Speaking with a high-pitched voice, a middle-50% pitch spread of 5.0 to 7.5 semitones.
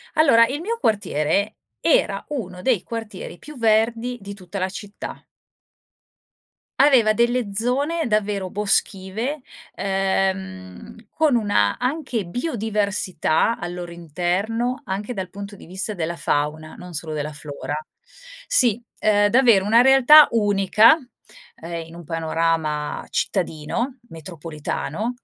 Yes: high, 200 Hz; wide, 5.5 semitones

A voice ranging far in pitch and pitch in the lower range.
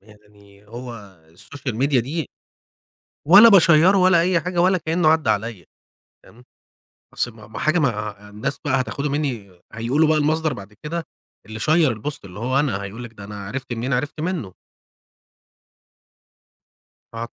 Yes: wide, 6.7 semitones; low, 130 Hz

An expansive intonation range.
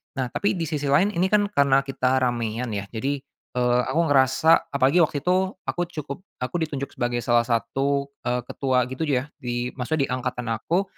No: average, 3.7 semitones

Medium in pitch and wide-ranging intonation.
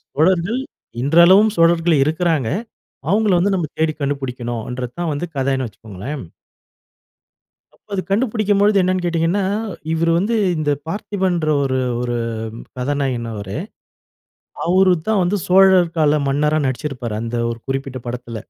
Yes: medium, 160 Hz; wide, 6.1 semitones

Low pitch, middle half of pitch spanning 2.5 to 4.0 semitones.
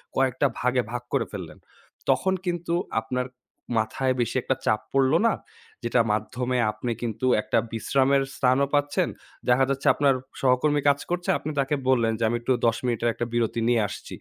Yes: low, 125 Hz; average, 2.9 semitones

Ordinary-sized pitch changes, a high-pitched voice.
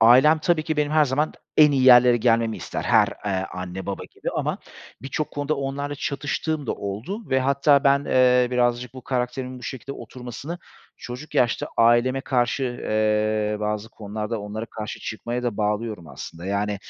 No: average, 4.3 semitones; low, 125 Hz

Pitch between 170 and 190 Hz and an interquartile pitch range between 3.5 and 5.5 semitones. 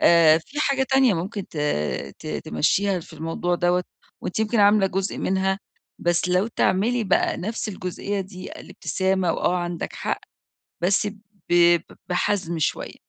No: medium, 185 Hz; average, 2.8 semitones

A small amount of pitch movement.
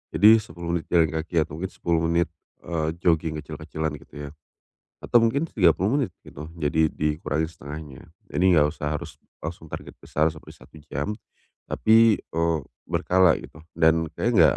Yes: narrow, 2.3 semitones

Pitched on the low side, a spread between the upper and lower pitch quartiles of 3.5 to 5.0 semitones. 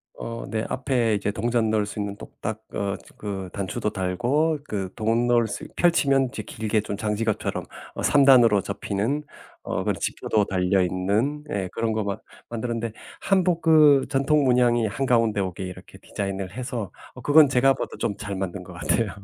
Yes: low, 110 Hz; average, 4.4 semitones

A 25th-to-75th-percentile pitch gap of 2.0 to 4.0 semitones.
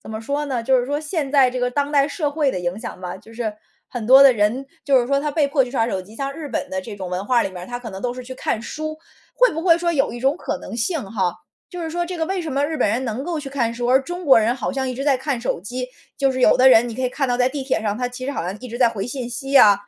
Yes: average, 3.7 semitones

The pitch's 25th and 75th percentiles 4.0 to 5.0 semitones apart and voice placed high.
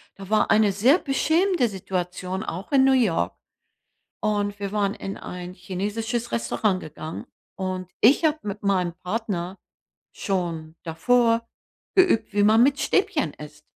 Yes: average, 4.4 semitones; high, 205 Hz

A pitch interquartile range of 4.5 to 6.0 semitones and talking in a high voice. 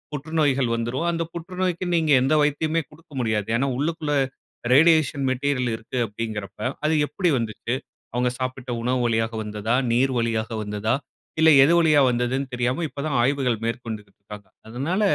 No: average, 4.9 semitones; low, 130 Hz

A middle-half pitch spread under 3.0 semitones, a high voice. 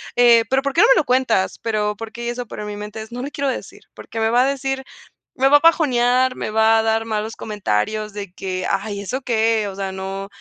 No: average, 3.3 semitones; high, 225 Hz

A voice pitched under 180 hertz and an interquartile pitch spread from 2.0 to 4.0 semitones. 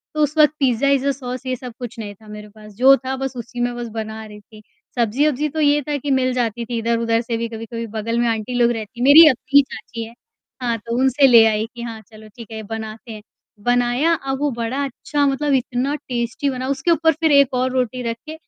No: high, 245 Hz; average, 3.1 semitones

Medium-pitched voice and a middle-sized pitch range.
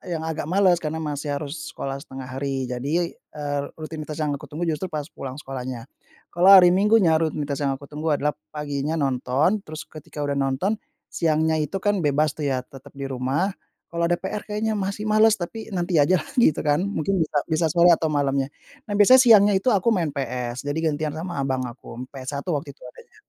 Yes: medium, 155 Hz; average, 4.0 semitones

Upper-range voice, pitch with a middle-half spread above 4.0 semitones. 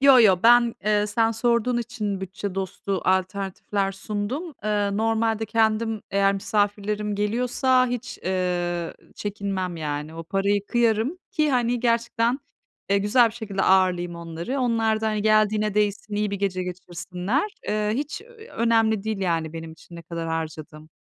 No: high, 210 Hz; average, 3.5 semitones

